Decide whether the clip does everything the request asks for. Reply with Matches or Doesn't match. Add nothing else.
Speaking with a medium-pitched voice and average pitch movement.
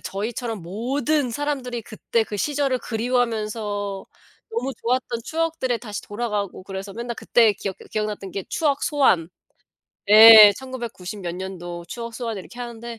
Doesn't match